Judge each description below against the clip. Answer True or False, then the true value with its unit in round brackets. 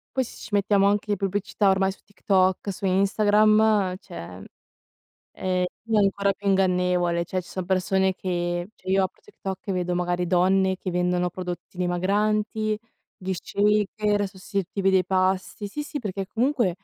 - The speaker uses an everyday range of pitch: False (2.1 semitones)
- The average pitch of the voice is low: False (190 Hz)